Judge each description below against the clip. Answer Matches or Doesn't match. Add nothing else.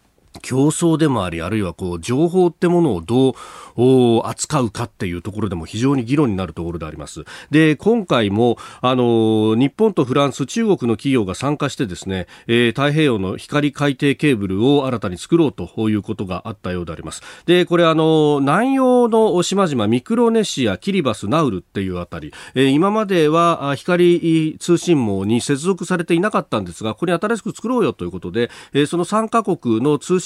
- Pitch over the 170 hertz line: Doesn't match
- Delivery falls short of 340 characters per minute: Doesn't match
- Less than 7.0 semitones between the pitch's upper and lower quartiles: Doesn't match